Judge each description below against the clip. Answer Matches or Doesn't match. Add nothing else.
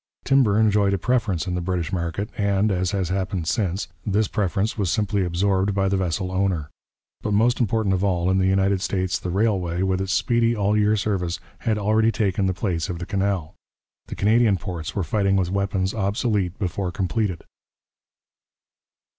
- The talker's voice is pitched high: Doesn't match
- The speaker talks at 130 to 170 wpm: Doesn't match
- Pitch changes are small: Matches